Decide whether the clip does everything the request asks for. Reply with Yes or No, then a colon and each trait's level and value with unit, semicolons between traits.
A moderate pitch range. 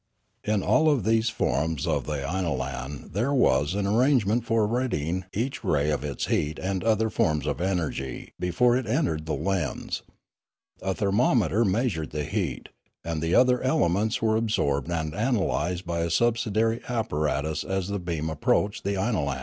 No: wide, 6.3 semitones